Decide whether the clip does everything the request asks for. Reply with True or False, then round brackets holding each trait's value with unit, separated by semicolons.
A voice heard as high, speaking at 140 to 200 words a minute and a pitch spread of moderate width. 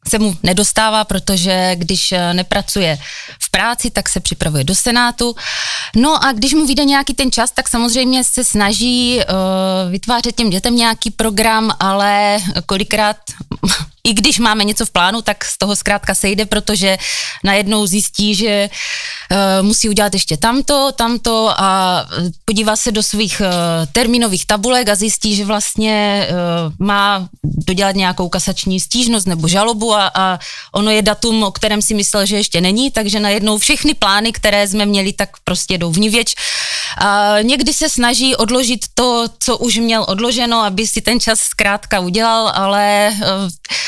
True (210 Hz; 155 wpm; 3.0 semitones)